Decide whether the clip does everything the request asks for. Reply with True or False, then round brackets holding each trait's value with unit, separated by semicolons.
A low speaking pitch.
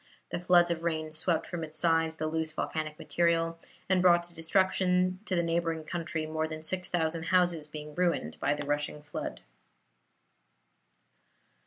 False (165 Hz)